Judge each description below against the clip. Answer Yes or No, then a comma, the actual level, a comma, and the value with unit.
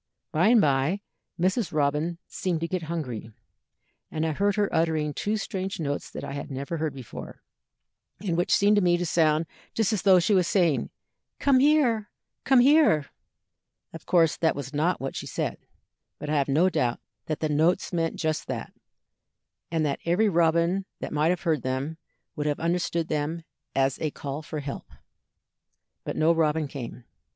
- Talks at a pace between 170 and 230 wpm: Yes, average, 180 wpm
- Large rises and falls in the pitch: No, average, 3.7 semitones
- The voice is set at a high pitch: No, medium, 165 Hz